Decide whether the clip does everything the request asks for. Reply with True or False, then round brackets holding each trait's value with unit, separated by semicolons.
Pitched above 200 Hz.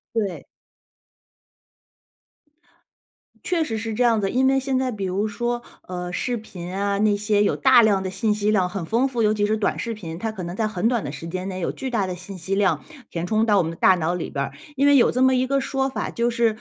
True (210 Hz)